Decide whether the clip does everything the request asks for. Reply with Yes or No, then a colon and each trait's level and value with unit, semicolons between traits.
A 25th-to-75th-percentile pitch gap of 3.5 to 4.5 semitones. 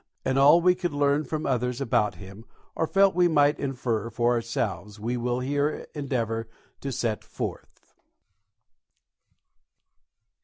Yes: average, 4.1 semitones